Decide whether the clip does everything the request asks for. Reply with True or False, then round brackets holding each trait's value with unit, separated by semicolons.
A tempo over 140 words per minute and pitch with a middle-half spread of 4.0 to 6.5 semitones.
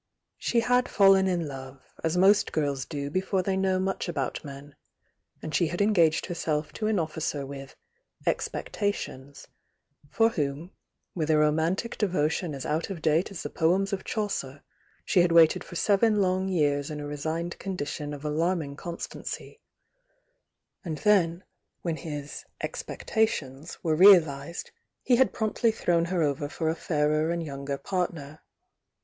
True (150 wpm; 4.3 semitones)